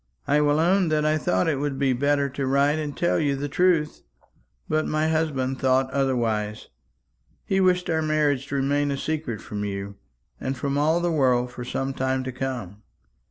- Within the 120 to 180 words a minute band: No, average, 190 wpm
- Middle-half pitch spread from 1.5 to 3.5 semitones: Yes, average, 2.9 semitones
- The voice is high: No, medium, 140 Hz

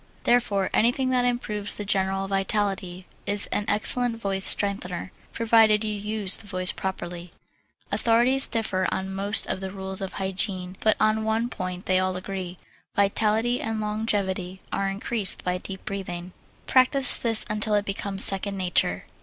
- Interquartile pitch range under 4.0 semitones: Yes, narrow, 2.5 semitones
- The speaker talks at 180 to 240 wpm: No, average, 155 wpm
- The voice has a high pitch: Yes, high, 200 Hz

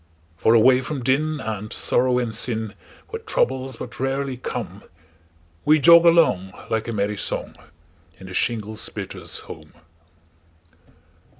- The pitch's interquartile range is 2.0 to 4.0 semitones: No, average, 4.6 semitones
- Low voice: Yes, low, 115 Hz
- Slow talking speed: Yes, slow, 115 wpm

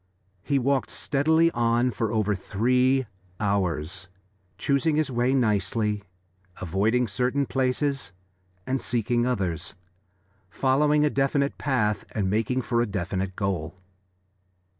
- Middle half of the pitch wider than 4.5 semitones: Yes, average, 4.9 semitones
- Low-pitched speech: Yes, low, 120 Hz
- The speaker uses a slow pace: Yes, slow, 115 wpm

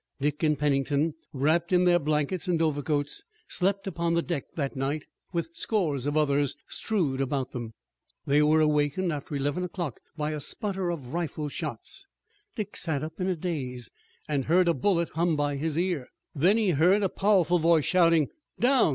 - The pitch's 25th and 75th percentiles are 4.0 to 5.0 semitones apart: No, average, 3.6 semitones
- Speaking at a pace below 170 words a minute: No, average, 175 wpm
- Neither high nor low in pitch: Yes, medium, 155 Hz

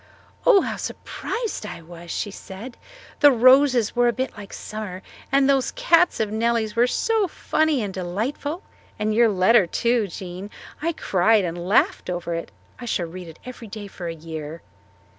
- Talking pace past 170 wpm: Yes, average, 180 wpm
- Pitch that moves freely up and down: Yes, wide, 5.9 semitones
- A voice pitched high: Yes, high, 215 Hz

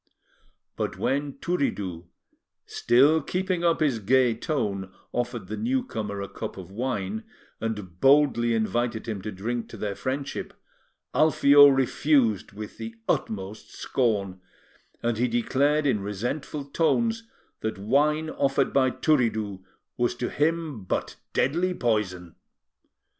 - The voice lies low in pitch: Yes, low, 120 Hz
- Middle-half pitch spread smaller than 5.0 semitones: No, wide, 5.5 semitones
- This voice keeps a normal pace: No, slow, 125 wpm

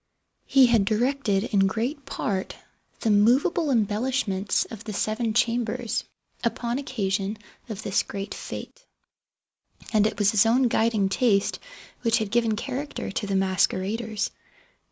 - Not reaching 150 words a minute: Yes, slow, 135 wpm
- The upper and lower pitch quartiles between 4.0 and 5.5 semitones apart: No, average, 3.1 semitones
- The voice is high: Yes, high, 220 Hz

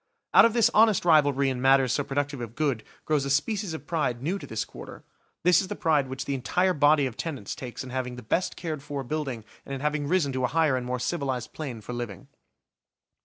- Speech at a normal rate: No, fast, 230 wpm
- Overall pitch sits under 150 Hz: Yes, medium, 140 Hz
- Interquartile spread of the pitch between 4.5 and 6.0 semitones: No, average, 3.8 semitones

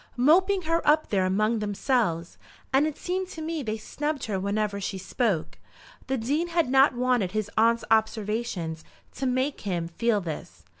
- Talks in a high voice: Yes, high, 230 Hz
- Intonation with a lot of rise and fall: Yes, wide, 6.2 semitones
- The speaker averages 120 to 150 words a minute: No, average, 165 wpm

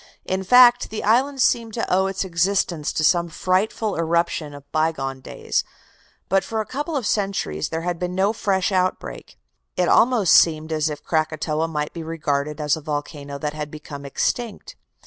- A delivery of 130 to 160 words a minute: No, average, 180 wpm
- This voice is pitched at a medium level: Yes, medium, 170 Hz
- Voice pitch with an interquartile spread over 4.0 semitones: Yes, average, 4.7 semitones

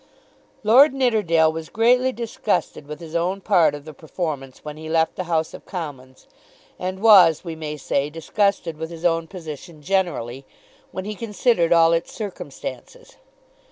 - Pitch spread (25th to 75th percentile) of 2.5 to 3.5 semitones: No, average, 4.3 semitones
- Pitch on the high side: No, medium, 165 Hz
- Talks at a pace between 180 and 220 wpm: No, average, 160 wpm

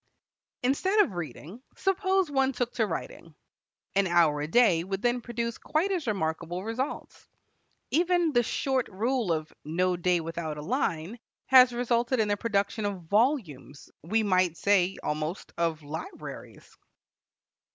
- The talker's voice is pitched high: Yes, high, 205 Hz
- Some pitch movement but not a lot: No, wide, 6.9 semitones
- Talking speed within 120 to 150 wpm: Yes, average, 140 wpm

